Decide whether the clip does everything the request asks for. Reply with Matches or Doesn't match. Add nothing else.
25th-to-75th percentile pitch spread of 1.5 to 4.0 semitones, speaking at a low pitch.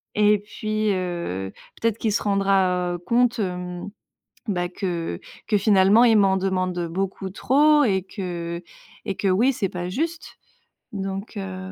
Doesn't match